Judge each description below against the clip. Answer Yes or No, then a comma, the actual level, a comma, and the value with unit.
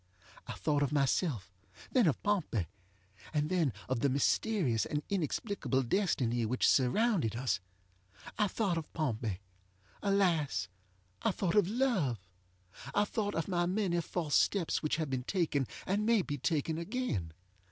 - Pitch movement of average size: No, wide, 7.7 semitones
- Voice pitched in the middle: Yes, medium, 155 Hz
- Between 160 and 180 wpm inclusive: No, average, 140 wpm